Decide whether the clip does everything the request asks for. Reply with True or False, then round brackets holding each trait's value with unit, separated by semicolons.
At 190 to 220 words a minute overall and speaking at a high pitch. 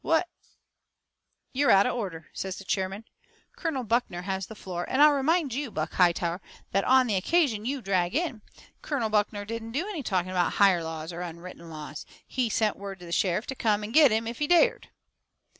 True (205 wpm; 210 Hz)